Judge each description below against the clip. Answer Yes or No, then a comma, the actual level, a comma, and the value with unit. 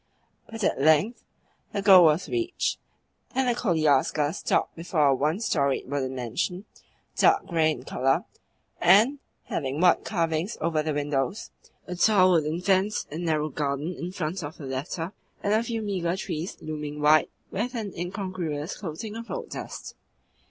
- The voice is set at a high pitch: No, medium, 170 Hz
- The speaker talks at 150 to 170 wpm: Yes, average, 160 wpm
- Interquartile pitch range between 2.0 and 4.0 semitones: No, average, 4.8 semitones